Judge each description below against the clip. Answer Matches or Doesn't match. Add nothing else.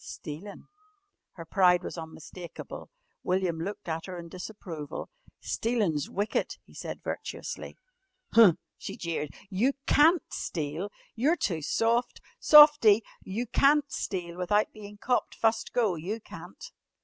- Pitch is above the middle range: Matches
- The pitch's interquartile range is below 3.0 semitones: Doesn't match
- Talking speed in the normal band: Doesn't match